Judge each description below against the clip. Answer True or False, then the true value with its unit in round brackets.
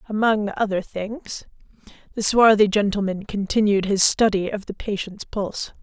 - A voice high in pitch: True (205 Hz)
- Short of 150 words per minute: True (135 wpm)